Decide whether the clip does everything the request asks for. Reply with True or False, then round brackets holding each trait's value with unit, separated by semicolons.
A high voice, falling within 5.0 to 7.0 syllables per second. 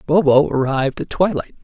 False (145 Hz; 5.6 syllables/s)